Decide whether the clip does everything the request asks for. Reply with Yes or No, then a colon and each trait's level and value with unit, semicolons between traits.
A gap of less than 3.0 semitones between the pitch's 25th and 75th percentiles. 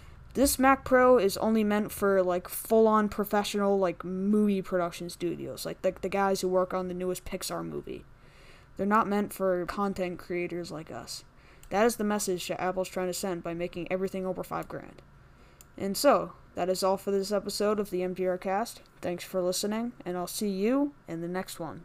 Yes: narrow, 2.5 semitones